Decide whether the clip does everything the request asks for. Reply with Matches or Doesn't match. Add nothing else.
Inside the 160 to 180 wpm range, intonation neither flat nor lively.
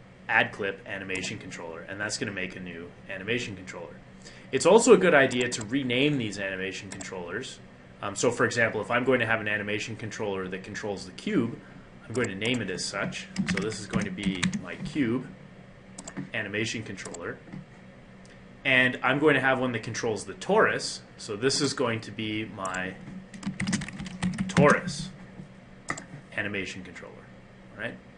Doesn't match